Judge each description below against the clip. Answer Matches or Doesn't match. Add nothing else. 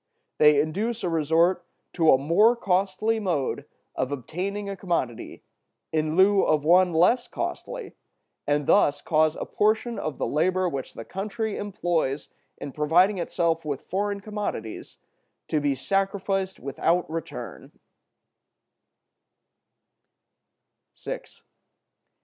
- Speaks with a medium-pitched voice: Matches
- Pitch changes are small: Doesn't match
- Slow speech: Matches